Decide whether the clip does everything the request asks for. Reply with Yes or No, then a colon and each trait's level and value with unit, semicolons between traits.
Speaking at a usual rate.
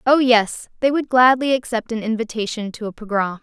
Yes: average, 195 wpm